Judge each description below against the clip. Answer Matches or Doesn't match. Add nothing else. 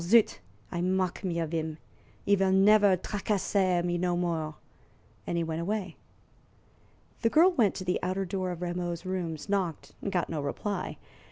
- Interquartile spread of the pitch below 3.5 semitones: Matches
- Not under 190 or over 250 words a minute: Doesn't match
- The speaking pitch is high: Doesn't match